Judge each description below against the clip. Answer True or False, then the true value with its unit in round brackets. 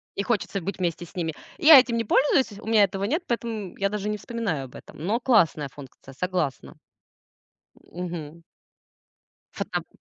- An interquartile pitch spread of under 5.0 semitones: False (5.4 semitones)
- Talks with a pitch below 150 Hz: False (200 Hz)